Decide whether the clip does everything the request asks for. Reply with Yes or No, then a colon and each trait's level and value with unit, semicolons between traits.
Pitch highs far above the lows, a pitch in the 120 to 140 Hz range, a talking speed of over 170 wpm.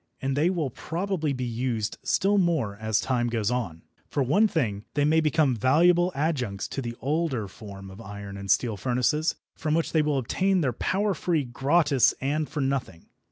Yes: wide, 5.9 semitones; low, 135 Hz; average, 185 wpm